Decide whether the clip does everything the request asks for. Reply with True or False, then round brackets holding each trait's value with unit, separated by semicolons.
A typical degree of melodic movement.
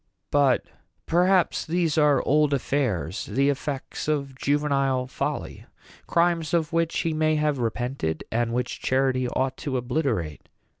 True (3.4 semitones)